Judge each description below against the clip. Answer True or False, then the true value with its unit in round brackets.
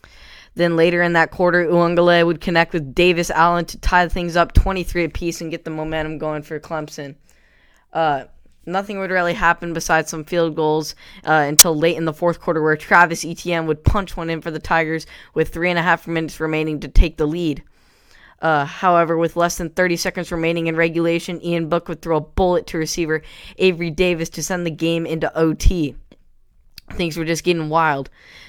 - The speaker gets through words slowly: False (195 wpm)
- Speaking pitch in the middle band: True (165 Hz)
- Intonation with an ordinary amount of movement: False (1.4 semitones)